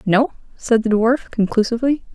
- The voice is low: No, high, 230 Hz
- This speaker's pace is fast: No, average, 140 wpm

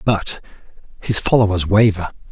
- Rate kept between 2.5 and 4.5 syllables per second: No, 4.8 syllables/s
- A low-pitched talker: Yes, low, 100 Hz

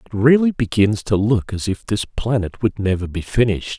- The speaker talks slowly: No, fast, 205 wpm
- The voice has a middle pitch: No, low, 110 Hz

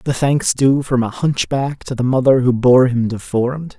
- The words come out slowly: No, fast, 205 wpm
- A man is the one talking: Yes, male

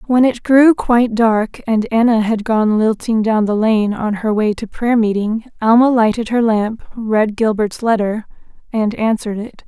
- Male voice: No, female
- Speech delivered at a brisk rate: No, average, 175 wpm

